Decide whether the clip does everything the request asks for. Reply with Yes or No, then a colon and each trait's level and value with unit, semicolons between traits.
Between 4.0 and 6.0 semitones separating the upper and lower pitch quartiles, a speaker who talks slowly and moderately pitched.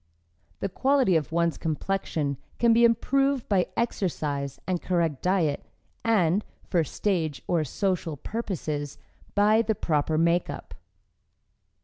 Yes: average, 5.3 semitones; slow, 115 wpm; medium, 180 Hz